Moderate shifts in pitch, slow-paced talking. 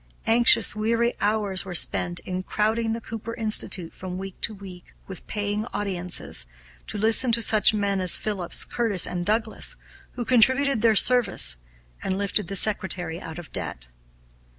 No: average, 3.4 semitones; average, 155 wpm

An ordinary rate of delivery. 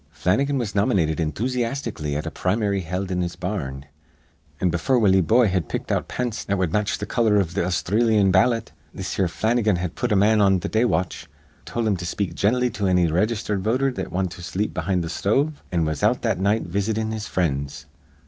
No: fast, 210 wpm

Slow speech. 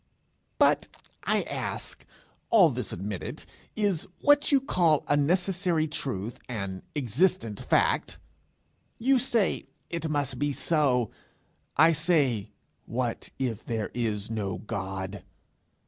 Yes: slow, 115 wpm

